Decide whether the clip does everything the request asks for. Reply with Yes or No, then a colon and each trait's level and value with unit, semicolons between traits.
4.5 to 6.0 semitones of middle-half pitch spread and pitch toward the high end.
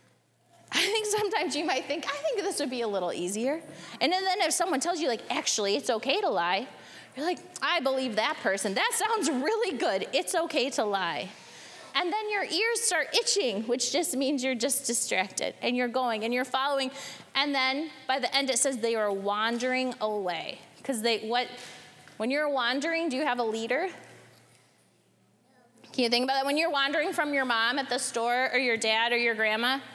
Yes: average, 5.1 semitones; very high, 265 Hz